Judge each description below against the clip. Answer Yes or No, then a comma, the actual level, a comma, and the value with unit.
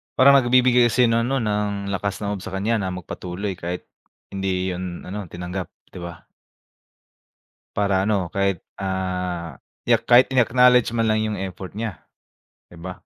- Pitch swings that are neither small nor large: Yes, average, 3.8 semitones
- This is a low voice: Yes, low, 100 Hz